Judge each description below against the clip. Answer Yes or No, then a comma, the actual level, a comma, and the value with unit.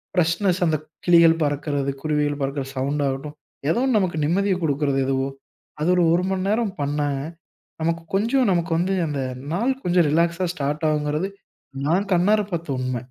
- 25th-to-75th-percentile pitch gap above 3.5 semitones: Yes, average, 4.0 semitones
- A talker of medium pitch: Yes, medium, 165 Hz